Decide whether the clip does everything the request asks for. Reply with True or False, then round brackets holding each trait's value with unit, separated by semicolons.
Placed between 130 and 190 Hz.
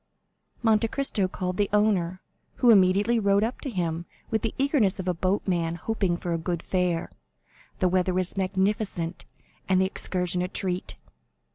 True (185 Hz)